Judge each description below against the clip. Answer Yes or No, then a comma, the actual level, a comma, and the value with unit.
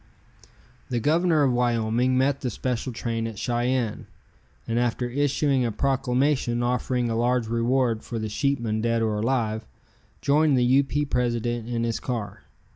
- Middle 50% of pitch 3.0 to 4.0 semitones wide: No, narrow, 2.4 semitones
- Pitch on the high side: No, low, 120 Hz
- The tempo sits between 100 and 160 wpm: Yes, average, 155 wpm